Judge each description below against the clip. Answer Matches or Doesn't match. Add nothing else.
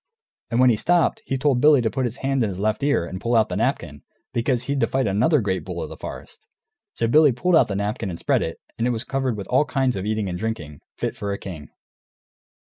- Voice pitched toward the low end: Matches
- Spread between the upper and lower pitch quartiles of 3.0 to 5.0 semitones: Matches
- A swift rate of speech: Matches